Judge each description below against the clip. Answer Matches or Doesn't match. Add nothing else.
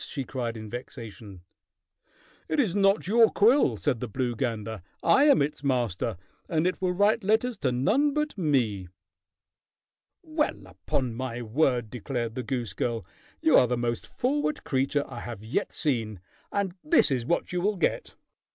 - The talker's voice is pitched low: Matches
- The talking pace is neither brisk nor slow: Matches